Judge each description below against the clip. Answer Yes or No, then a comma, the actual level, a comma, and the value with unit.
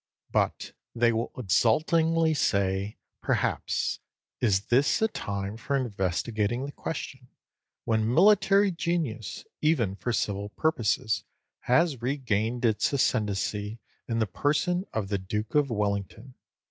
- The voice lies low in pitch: Yes, low, 115 Hz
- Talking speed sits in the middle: No, slow, 120 wpm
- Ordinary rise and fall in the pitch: No, wide, 5.9 semitones